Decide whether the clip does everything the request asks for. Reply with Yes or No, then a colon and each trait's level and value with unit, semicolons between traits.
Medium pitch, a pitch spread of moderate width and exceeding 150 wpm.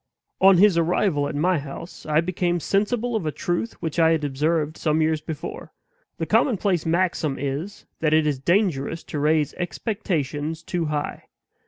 Yes: medium, 165 Hz; average, 3.3 semitones; average, 165 wpm